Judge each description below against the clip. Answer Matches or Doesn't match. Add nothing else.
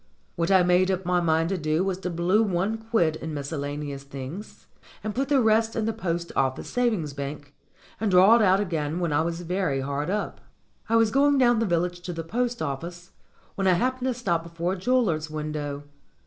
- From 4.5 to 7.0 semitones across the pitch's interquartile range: Matches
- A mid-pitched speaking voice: Matches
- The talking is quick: Matches